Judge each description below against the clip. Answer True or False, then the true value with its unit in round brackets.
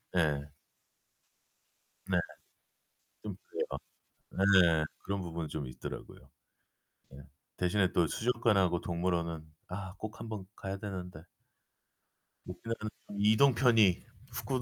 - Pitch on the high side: False (95 Hz)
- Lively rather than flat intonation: False (4.2 semitones)